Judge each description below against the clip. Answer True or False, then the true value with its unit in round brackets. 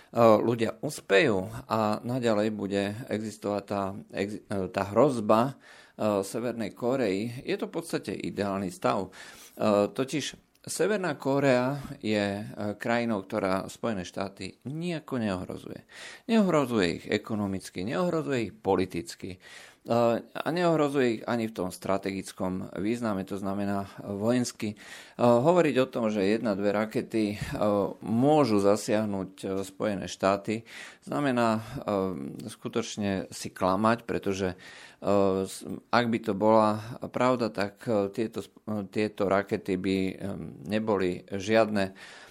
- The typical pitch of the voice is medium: False (105 Hz)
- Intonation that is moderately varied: True (3.4 semitones)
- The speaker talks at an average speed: False (100 wpm)